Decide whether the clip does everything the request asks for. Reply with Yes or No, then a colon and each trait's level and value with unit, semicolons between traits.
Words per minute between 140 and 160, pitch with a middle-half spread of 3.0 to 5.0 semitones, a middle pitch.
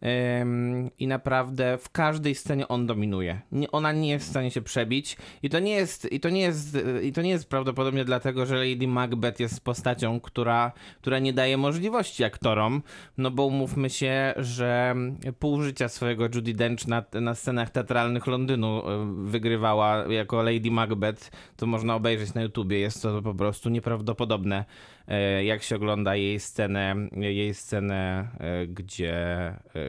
No: average, 155 wpm; average, 3.7 semitones; low, 120 Hz